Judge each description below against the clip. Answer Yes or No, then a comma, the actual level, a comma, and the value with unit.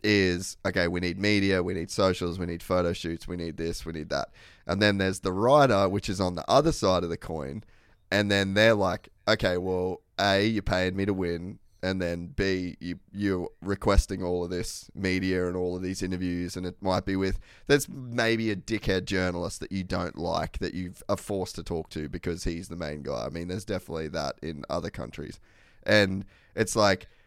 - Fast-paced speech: Yes, fast, 210 wpm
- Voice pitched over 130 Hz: No, very low, 95 Hz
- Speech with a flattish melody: Yes, narrow, 2.3 semitones